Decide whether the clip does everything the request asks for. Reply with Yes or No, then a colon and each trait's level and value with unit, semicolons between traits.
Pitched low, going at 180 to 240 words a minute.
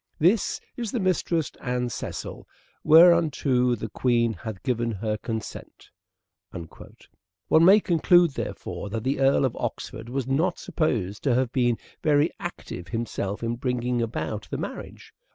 No: low, 125 Hz; slow, 135 wpm